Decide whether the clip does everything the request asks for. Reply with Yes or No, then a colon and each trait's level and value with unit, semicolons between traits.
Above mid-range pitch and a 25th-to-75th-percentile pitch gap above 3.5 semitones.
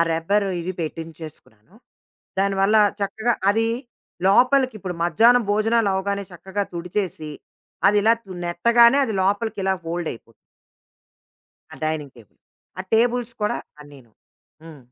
Yes: high, 195 Hz; average, 5.3 semitones